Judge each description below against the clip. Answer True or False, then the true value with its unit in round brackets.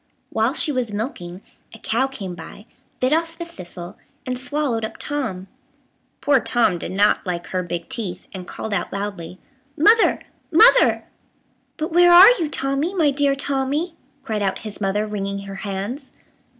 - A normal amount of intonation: False (6.8 semitones)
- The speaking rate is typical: True (165 wpm)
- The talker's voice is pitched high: True (230 Hz)